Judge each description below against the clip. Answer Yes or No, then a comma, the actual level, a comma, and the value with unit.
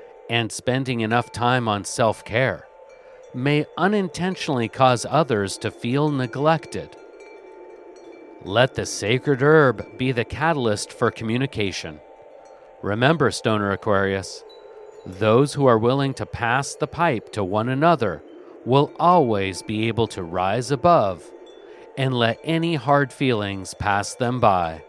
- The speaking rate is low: Yes, slow, 125 wpm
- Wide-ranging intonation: Yes, wide, 7.2 semitones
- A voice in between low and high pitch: No, low, 130 Hz